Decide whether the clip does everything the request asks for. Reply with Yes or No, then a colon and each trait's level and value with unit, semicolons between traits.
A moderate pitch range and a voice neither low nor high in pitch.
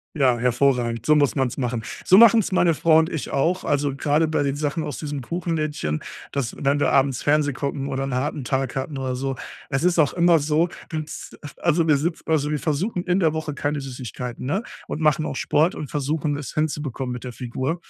Yes: average, 3.0 semitones; medium, 145 Hz